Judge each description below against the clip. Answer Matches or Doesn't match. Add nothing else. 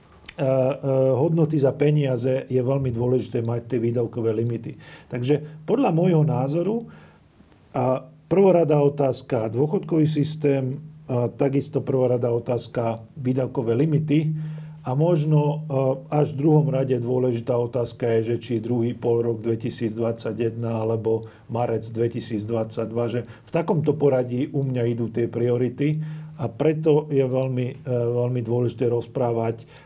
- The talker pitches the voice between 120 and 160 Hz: Matches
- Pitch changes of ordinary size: Matches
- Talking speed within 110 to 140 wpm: Matches